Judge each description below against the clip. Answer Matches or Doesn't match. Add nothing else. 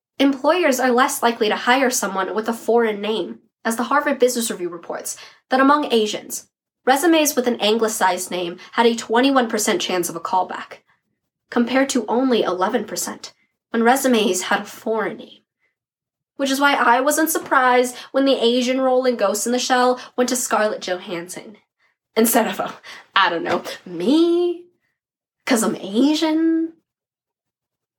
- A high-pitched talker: Matches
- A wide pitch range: Doesn't match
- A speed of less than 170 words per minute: Matches